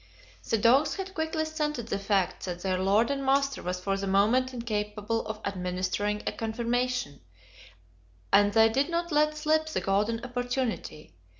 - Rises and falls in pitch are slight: No, wide, 5.5 semitones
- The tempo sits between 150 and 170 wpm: Yes, average, 160 wpm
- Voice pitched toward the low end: No, high, 230 Hz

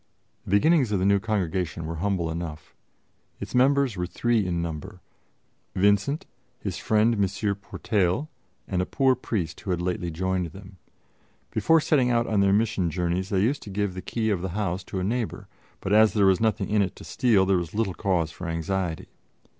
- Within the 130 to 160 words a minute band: No, average, 195 wpm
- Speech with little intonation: No, average, 3.5 semitones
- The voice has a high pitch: No, very low, 95 Hz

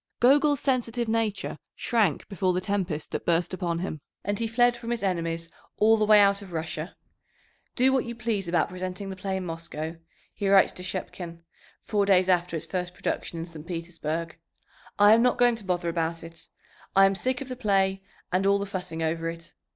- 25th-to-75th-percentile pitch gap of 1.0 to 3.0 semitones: No, average, 4.2 semitones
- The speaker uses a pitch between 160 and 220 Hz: Yes, high, 190 Hz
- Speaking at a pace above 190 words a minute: Yes, average, 200 wpm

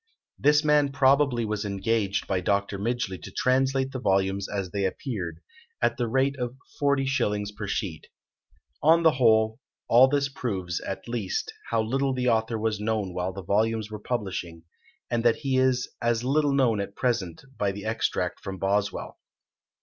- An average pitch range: Yes, average, 4.7 semitones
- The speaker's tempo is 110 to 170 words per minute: Yes, average, 165 wpm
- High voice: No, low, 110 Hz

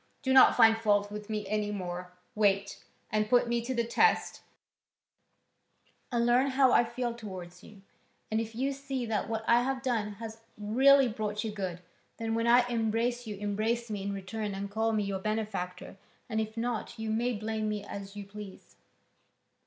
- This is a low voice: No, high, 220 Hz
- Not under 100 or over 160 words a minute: No, average, 185 wpm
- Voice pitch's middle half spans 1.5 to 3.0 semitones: Yes, narrow, 2.5 semitones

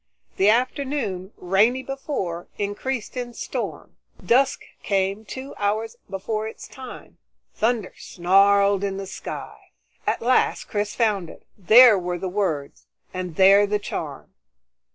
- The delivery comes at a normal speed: No, slow, 130 wpm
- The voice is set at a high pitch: Yes, high, 205 Hz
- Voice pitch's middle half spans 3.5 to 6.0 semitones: Yes, average, 3.9 semitones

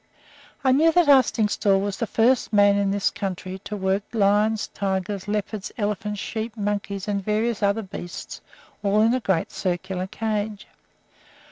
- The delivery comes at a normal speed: Yes, average, 150 wpm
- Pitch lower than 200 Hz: No, high, 205 Hz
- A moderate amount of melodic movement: No, narrow, 2.0 semitones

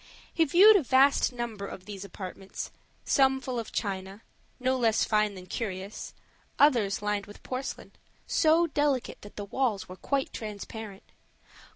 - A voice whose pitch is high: Yes, high, 225 Hz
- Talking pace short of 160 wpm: Yes, average, 150 wpm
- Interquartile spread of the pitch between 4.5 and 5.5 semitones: Yes, average, 5.0 semitones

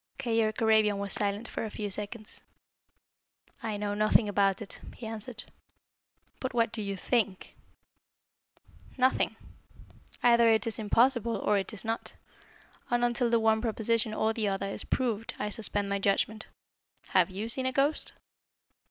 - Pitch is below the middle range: No, high, 220 Hz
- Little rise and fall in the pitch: Yes, narrow, 2.2 semitones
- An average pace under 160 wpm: Yes, average, 150 wpm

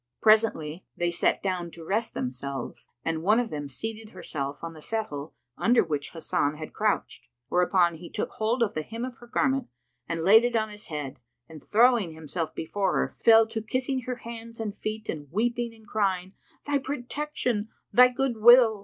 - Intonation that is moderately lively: No, wide, 6.2 semitones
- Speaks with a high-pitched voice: Yes, high, 215 Hz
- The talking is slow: No, average, 185 wpm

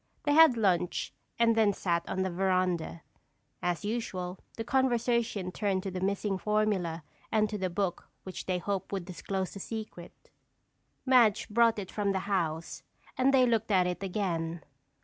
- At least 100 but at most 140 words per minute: No, average, 165 wpm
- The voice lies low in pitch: No, high, 195 Hz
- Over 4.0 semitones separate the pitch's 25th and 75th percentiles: No, average, 3.5 semitones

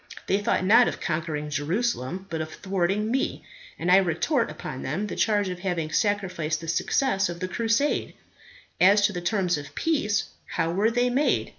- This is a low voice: No, high, 190 Hz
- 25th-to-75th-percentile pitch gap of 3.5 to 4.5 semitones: Yes, average, 4.2 semitones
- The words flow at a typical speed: Yes, average, 180 wpm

